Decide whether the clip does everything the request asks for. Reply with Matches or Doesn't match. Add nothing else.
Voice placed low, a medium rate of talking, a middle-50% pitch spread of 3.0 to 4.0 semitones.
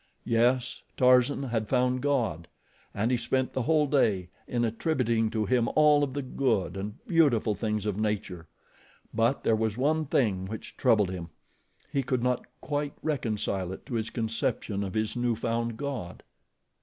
Matches